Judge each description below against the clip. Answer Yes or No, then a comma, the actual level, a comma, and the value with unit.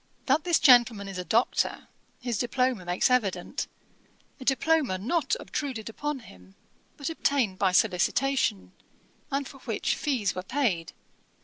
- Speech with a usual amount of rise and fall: No, wide, 6.5 semitones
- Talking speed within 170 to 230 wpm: No, slow, 135 wpm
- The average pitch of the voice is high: Yes, high, 245 Hz